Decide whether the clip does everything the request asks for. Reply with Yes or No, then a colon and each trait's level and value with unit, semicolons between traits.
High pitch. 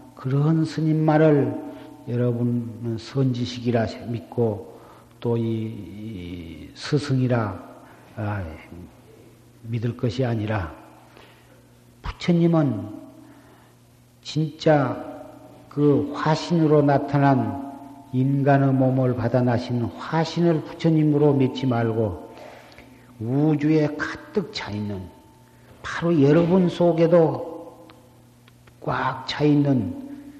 No: low, 130 Hz